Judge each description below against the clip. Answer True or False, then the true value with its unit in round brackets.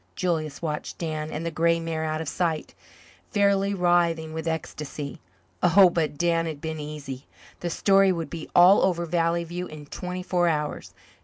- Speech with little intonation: True (2.1 semitones)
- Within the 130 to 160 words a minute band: False (170 wpm)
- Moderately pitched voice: True (165 Hz)